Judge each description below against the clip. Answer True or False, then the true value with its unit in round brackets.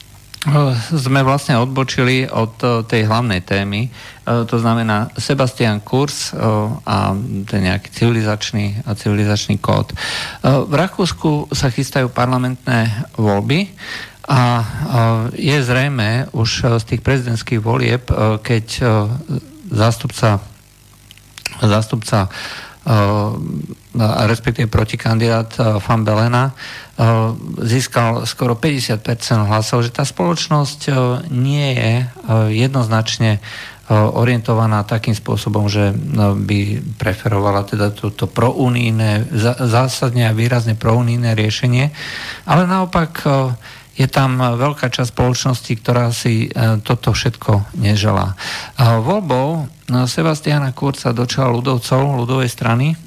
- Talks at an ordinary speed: False (95 wpm)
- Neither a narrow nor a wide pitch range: True (3.1 semitones)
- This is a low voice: True (120 Hz)